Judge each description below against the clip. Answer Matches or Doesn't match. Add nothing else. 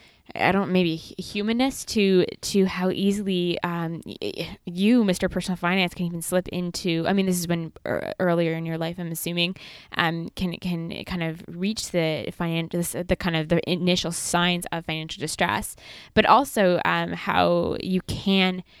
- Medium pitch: Matches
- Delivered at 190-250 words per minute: Doesn't match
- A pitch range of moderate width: Doesn't match